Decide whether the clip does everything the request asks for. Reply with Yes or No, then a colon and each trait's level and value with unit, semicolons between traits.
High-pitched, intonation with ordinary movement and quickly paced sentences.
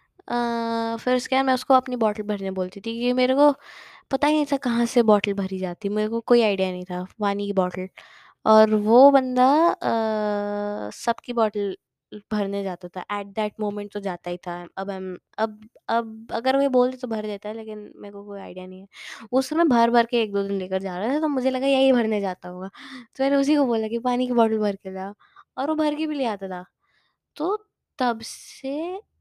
Yes: high, 220 Hz; average, 4.2 semitones; fast, 220 wpm